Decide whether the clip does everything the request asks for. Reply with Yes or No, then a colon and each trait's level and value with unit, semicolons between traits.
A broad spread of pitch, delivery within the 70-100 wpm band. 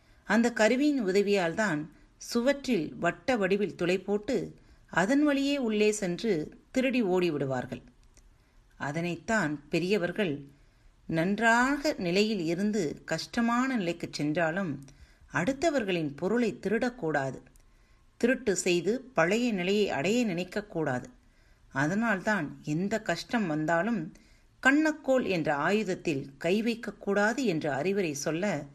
Yes: wide, 6.3 semitones; average, 90 wpm